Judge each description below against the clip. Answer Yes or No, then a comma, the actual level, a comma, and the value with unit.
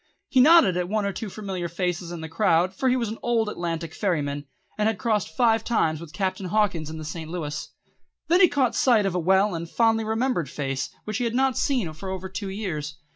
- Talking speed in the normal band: No, fast, 230 wpm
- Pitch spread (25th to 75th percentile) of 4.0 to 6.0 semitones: Yes, average, 5.2 semitones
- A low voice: No, high, 190 Hz